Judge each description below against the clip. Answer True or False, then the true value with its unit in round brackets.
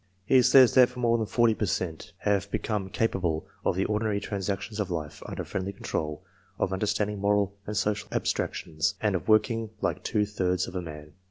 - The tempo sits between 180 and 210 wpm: True (185 wpm)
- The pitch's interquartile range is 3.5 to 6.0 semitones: False (2.7 semitones)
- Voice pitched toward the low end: True (100 Hz)